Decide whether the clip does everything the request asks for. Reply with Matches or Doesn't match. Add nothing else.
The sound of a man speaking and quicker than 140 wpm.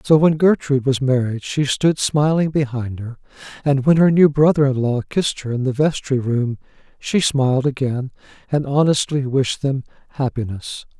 Matches